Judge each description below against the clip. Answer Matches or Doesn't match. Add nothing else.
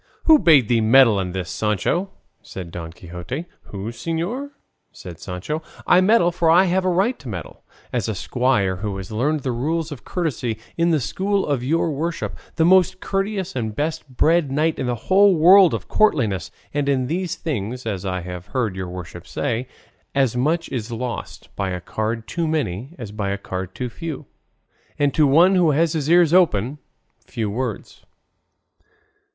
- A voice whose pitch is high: Doesn't match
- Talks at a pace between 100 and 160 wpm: Doesn't match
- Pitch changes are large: Matches